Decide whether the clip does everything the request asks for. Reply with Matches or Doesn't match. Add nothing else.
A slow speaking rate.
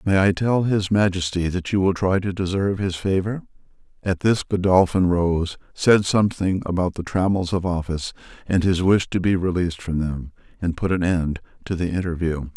Doesn't match